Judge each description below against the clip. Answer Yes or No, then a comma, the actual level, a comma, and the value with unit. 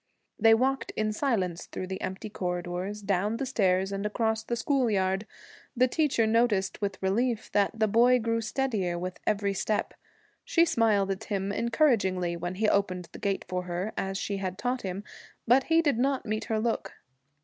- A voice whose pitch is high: Yes, high, 210 Hz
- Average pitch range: Yes, average, 3.6 semitones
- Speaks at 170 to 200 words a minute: Yes, average, 180 wpm